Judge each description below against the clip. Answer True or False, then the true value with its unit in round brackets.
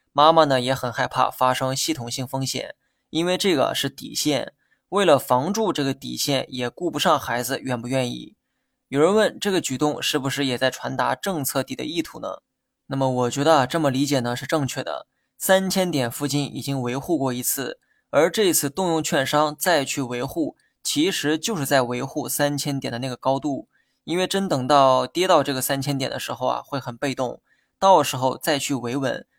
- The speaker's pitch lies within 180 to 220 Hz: False (140 Hz)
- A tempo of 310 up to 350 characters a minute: False (285 characters per minute)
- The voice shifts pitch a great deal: False (3.4 semitones)